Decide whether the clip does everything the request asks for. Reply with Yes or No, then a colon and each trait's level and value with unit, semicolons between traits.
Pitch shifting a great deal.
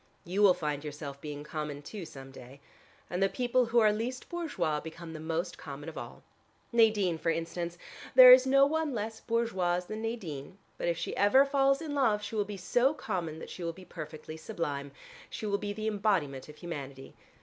Yes: wide, 6.6 semitones